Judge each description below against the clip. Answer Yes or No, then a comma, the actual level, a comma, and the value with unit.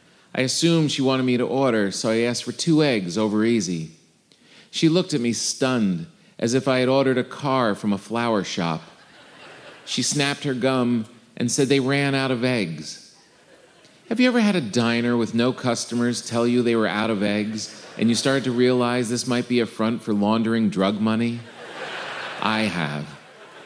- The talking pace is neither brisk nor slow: Yes, average, 190 wpm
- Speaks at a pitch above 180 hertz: No, low, 120 Hz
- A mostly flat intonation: No, average, 3.3 semitones